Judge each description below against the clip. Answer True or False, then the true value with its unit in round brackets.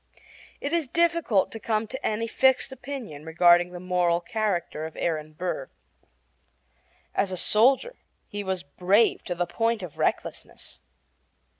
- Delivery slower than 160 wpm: True (140 wpm)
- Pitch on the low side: False (200 Hz)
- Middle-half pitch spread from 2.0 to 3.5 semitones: False (5.1 semitones)